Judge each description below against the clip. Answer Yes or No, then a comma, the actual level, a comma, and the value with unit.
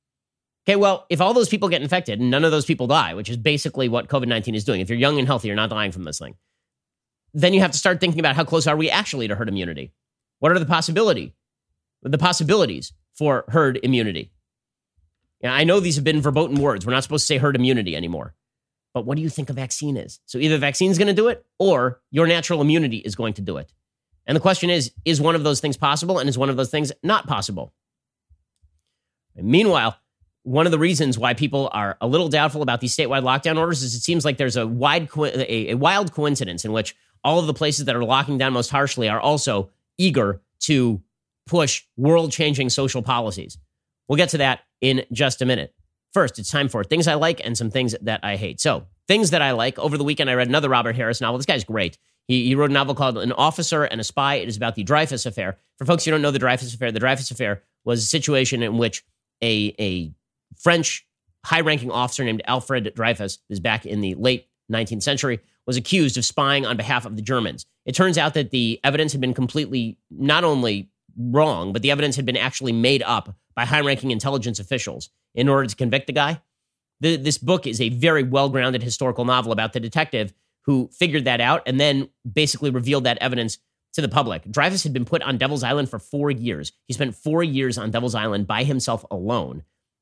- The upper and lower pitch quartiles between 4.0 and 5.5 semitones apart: Yes, average, 4.7 semitones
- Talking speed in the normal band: No, fast, 225 wpm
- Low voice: Yes, low, 130 Hz